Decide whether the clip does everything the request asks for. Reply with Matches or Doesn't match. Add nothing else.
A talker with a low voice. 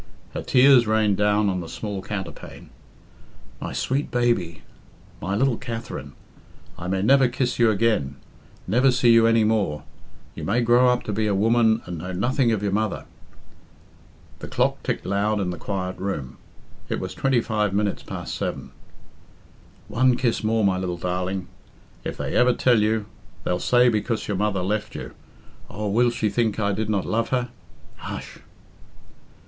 Matches